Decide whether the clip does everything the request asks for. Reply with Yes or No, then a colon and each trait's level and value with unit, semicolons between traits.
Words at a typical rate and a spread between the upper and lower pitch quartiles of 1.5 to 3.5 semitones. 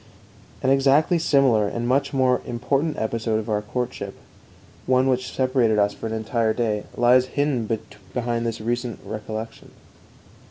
Yes: average, 145 wpm; average, 2.9 semitones